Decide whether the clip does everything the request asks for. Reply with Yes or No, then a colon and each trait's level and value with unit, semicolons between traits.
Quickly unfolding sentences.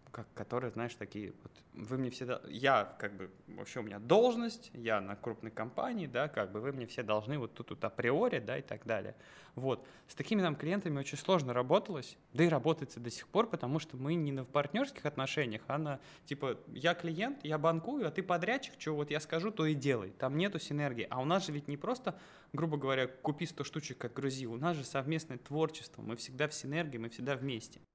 Yes: fast, 215 wpm